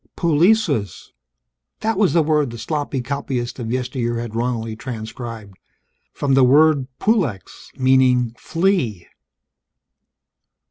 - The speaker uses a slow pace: Yes, slow, 105 wpm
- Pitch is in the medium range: No, low, 130 Hz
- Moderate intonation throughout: Yes, average, 4.7 semitones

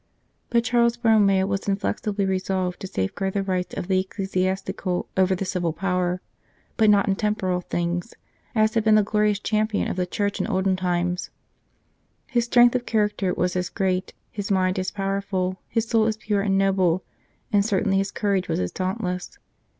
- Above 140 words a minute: Yes, average, 180 wpm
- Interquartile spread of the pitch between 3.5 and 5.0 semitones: No, narrow, 2.4 semitones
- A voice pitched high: Yes, high, 195 Hz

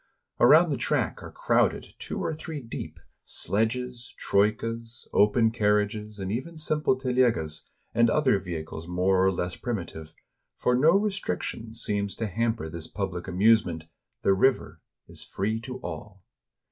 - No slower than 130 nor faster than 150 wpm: Yes, average, 140 wpm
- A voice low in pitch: Yes, low, 110 Hz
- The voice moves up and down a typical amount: Yes, average, 4.6 semitones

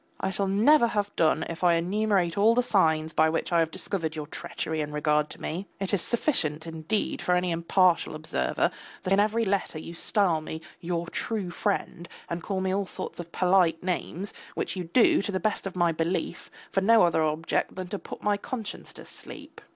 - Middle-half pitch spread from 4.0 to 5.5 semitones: No, average, 3.5 semitones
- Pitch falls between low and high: Yes, medium, 180 Hz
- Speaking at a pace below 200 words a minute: No, fast, 205 wpm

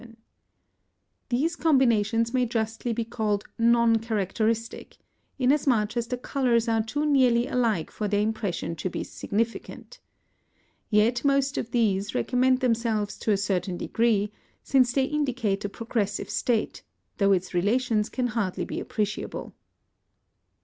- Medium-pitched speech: No, high, 230 Hz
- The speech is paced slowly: Yes, slow, 130 wpm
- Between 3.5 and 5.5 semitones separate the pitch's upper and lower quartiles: No, average, 3.1 semitones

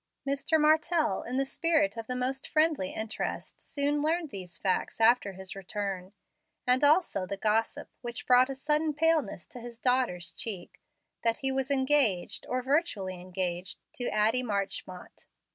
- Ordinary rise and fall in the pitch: No, wide, 6.6 semitones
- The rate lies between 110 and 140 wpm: No, average, 155 wpm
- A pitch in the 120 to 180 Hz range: No, very high, 250 Hz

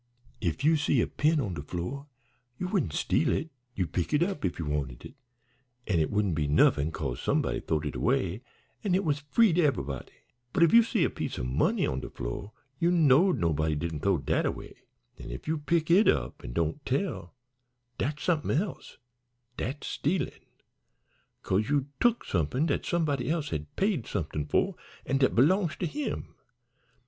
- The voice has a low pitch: Yes, low, 130 Hz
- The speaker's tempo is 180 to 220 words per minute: Yes, average, 185 wpm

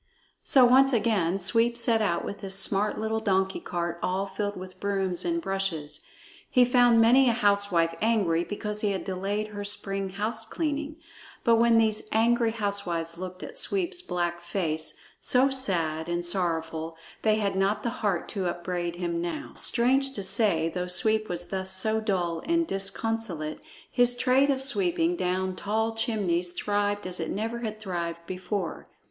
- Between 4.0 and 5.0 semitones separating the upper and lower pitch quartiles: Yes, average, 4.3 semitones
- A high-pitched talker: Yes, high, 200 Hz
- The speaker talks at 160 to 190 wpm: Yes, average, 165 wpm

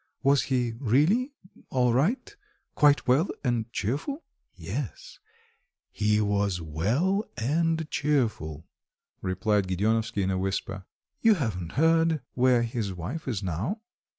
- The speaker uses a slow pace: Yes, slow, 120 wpm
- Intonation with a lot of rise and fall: Yes, wide, 7.6 semitones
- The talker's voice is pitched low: Yes, low, 120 Hz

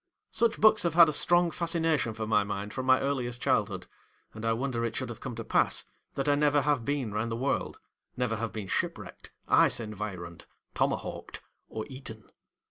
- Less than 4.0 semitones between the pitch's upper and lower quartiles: No, average, 4.8 semitones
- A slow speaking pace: No, average, 190 wpm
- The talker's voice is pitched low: Yes, low, 125 Hz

